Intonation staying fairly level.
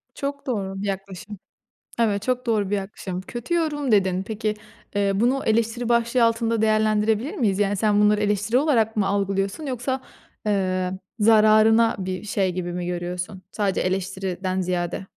No: average, 3.1 semitones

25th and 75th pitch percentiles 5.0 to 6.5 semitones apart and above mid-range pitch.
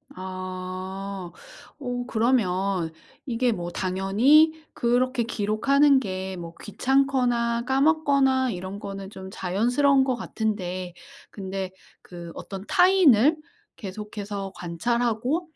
Yes: wide, 5.6 semitones; high, 220 Hz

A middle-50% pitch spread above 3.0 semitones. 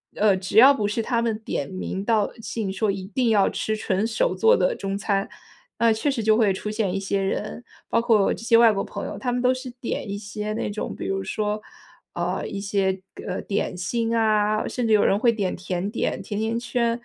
No: average, 2.7 semitones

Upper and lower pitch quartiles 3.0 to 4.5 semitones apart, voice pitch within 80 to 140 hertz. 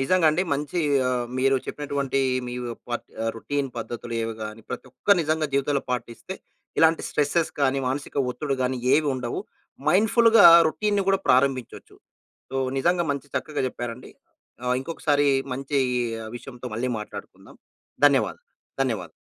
Yes: average, 3.6 semitones; low, 135 Hz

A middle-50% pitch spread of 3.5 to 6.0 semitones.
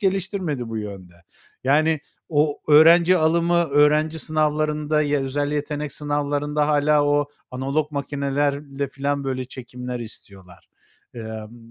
No: narrow, 2.4 semitones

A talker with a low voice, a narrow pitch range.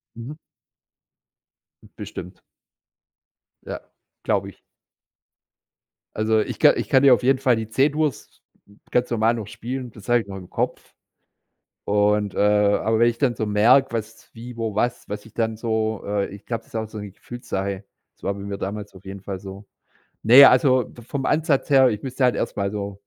No: low, 110 Hz; average, 3.2 semitones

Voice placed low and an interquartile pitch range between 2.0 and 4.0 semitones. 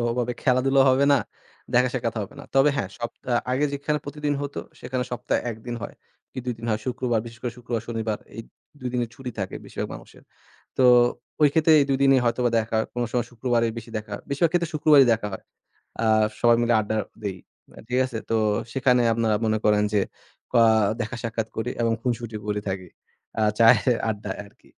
Yes: low, 120 Hz; narrow, 2.6 semitones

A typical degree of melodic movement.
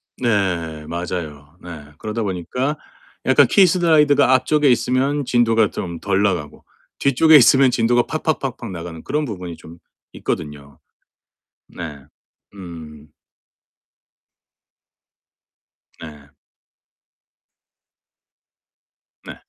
No: wide, 8.4 semitones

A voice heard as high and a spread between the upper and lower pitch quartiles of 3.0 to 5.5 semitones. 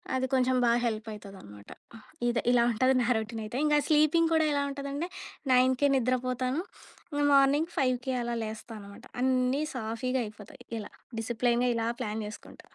Yes: very high, 250 Hz; average, 3.3 semitones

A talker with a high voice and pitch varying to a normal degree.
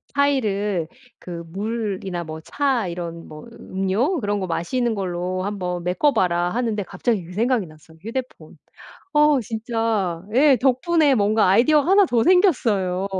No: high, 210 Hz; wide, 6.0 semitones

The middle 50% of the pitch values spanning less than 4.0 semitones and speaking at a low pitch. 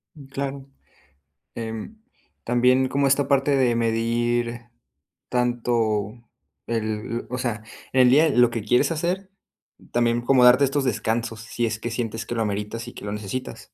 Yes: narrow, 2.6 semitones; low, 120 Hz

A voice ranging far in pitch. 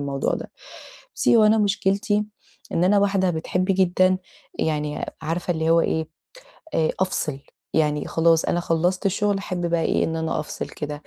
No: average, 3.2 semitones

